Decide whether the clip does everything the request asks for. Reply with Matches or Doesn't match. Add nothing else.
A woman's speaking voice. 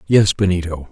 Doesn't match